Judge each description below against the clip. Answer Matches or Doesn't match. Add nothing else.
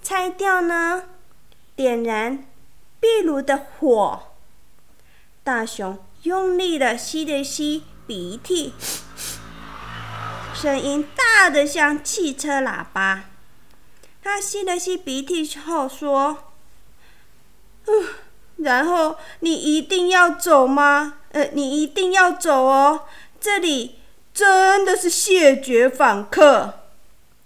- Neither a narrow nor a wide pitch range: Matches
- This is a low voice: Doesn't match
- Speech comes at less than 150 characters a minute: Matches